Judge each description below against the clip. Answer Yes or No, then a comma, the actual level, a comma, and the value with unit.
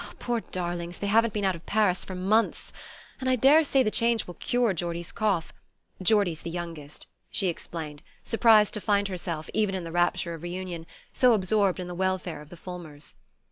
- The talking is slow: No, average, 185 wpm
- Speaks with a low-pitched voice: No, medium, 185 Hz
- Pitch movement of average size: Yes, average, 3.9 semitones